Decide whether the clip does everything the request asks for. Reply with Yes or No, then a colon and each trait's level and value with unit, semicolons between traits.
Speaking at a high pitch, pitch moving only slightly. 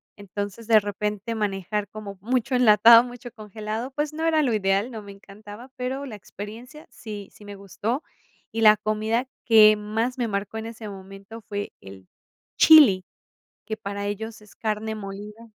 Yes: high, 215 Hz; narrow, 2.3 semitones